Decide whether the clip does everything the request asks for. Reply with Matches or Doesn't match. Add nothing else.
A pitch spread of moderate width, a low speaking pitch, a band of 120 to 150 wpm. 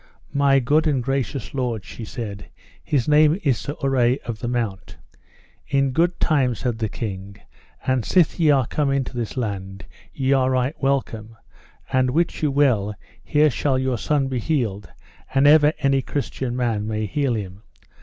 Doesn't match